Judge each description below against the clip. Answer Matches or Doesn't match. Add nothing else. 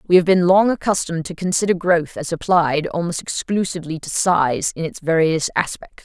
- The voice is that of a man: Doesn't match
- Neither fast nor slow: Matches